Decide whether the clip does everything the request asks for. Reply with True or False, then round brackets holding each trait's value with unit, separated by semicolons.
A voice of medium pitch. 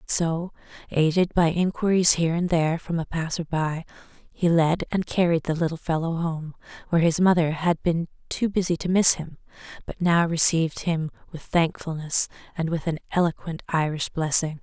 True (165 Hz)